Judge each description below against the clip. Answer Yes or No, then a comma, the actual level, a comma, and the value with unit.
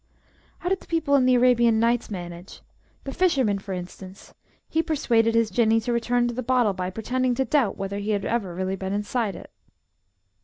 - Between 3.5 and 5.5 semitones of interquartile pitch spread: Yes, average, 4.3 semitones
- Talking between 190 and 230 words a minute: Yes, average, 195 wpm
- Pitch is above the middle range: Yes, high, 230 Hz